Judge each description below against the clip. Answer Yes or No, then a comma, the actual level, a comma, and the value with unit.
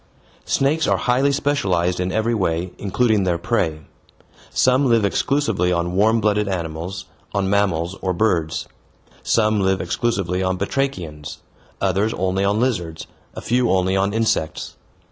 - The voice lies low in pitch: Yes, low, 100 Hz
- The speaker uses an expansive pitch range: No, average, 4.1 semitones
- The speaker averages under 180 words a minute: Yes, average, 140 wpm